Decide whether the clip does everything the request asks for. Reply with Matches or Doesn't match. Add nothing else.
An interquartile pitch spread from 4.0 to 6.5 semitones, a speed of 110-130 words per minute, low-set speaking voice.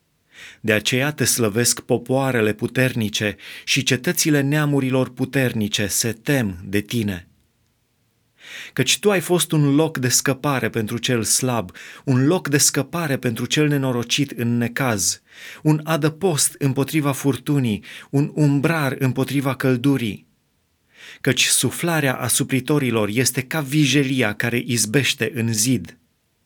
Doesn't match